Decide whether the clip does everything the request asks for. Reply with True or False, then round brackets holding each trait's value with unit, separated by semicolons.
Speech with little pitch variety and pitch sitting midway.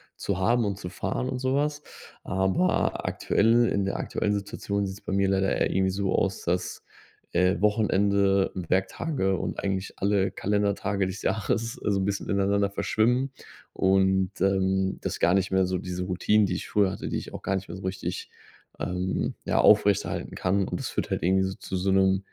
False (1.3 semitones; 95 Hz)